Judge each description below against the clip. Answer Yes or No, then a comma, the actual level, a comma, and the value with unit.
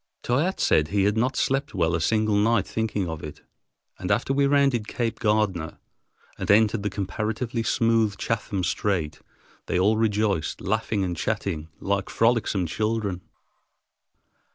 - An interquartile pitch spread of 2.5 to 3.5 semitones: Yes, average, 3.0 semitones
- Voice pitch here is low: Yes, low, 105 Hz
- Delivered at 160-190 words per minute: No, average, 145 wpm